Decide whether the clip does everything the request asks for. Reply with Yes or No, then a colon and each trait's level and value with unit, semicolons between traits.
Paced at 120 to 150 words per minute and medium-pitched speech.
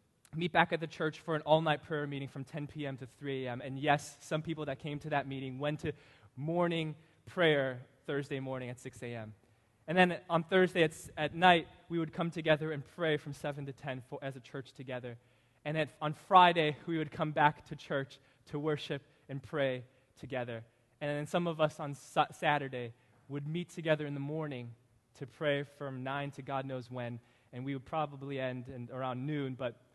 No: fast, 205 wpm; medium, 145 Hz